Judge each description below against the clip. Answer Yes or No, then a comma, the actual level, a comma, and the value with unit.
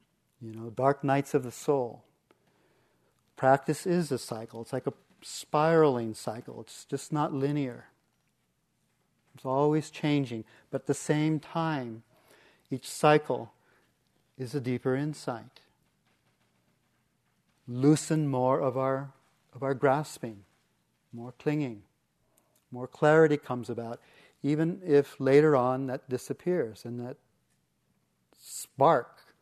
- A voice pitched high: No, low, 135 Hz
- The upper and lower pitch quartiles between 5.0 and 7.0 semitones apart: No, average, 3.2 semitones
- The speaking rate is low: Yes, slow, 115 wpm